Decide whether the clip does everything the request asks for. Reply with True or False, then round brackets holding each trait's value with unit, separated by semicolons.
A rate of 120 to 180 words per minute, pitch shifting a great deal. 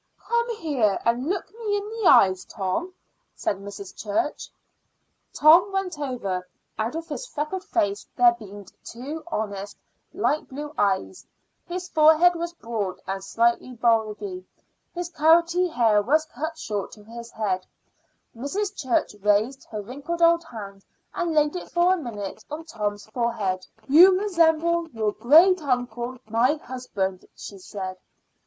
True (145 wpm; 8.3 semitones)